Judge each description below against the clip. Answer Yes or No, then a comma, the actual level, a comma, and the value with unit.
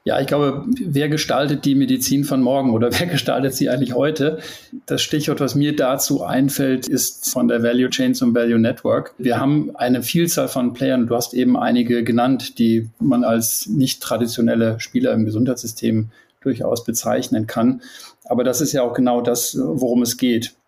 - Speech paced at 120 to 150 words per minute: No, average, 175 wpm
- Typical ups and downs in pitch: Yes, average, 3.2 semitones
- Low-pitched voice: Yes, low, 125 Hz